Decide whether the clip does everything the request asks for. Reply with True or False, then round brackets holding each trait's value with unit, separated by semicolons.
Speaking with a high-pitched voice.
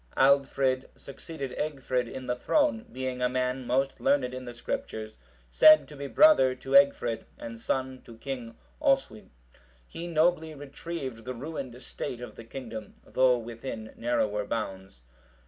False (130 Hz)